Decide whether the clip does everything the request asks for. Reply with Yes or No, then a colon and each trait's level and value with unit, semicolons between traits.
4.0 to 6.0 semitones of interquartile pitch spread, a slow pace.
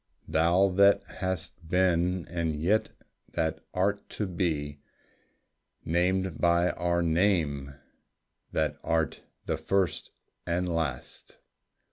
No: narrow, 2.4 semitones; slow, 100 wpm